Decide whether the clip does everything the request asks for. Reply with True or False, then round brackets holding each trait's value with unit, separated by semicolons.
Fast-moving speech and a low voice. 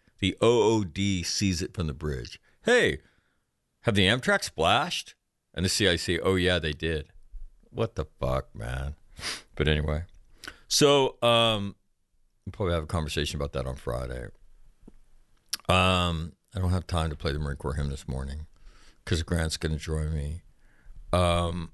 False (150 wpm; 80 Hz)